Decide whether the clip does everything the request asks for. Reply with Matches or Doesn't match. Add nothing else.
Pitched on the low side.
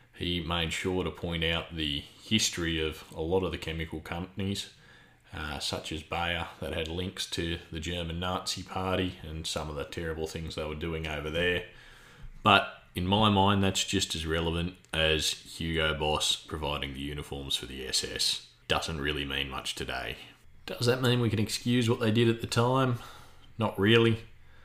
Matches